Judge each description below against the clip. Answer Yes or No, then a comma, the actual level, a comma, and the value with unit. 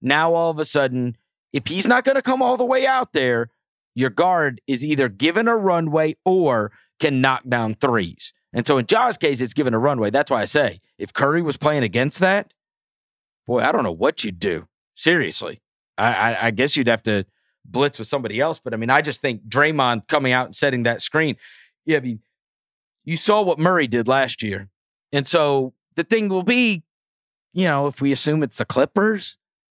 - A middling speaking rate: No, fast, 210 wpm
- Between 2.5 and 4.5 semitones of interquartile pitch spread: No, wide, 5.4 semitones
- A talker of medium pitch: Yes, medium, 145 Hz